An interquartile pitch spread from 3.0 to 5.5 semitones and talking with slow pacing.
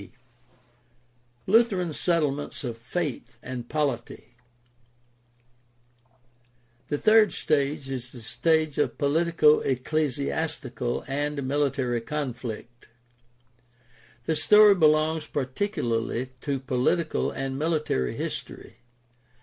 Yes: average, 4.3 semitones; slow, 95 wpm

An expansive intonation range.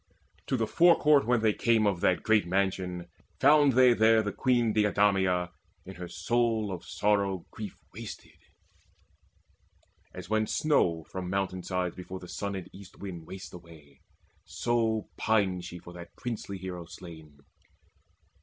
No: average, 3.7 semitones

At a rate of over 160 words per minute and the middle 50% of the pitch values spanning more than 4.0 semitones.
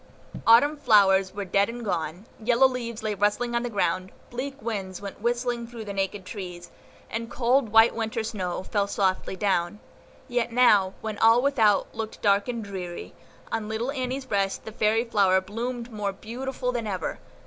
No: average, 170 wpm; average, 3.3 semitones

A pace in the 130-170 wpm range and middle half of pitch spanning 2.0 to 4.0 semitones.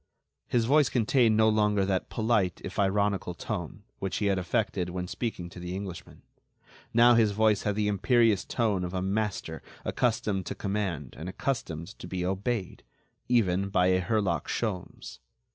Yes: average, 160 wpm; average, 3.1 semitones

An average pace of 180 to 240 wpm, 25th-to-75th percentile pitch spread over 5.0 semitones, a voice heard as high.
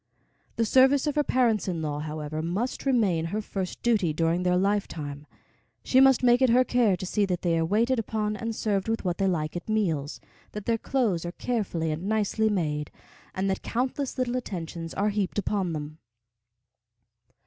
Yes: average, 185 wpm; wide, 5.6 semitones; high, 200 Hz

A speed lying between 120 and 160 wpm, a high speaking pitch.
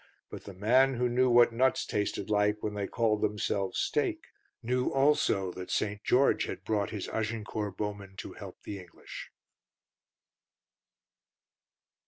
No: average, 140 wpm; low, 105 Hz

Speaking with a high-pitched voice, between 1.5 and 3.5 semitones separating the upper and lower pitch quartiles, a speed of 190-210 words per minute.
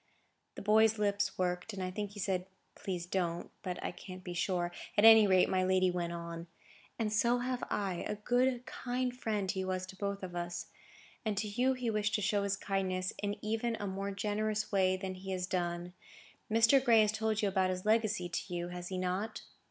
Yes: high, 195 Hz; average, 2.9 semitones; fast, 205 wpm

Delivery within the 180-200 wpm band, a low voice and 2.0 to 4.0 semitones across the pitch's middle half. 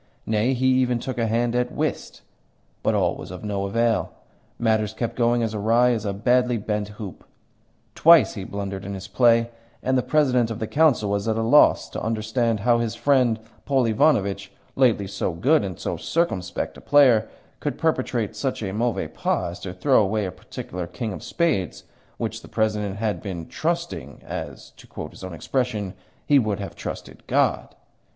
Yes: average, 185 wpm; low, 110 Hz; average, 3.5 semitones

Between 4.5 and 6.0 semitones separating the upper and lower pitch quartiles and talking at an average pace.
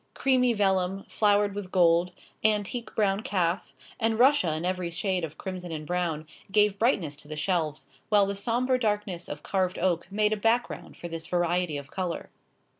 No: average, 3.6 semitones; average, 175 wpm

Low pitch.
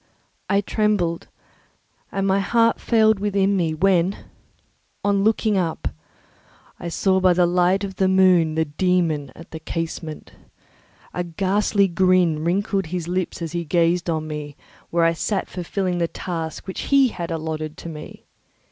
No: medium, 180 Hz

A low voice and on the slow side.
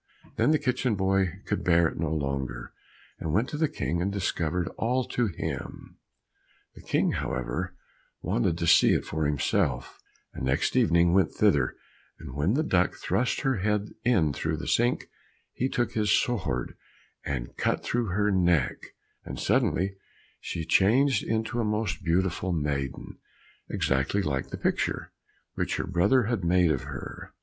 No: very low, 95 Hz; average, 160 wpm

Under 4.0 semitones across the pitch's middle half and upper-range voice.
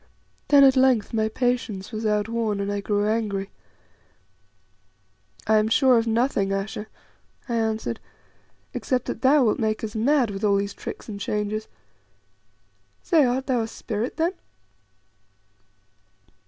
Yes: average, 3.0 semitones; high, 220 Hz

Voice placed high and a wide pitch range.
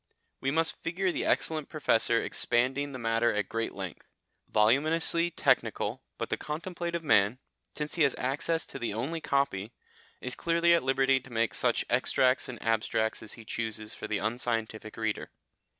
No: low, 130 Hz; wide, 5.8 semitones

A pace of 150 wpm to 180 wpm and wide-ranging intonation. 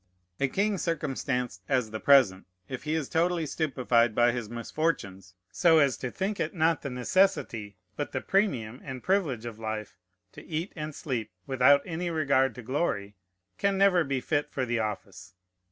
Yes: average, 170 wpm; wide, 5.7 semitones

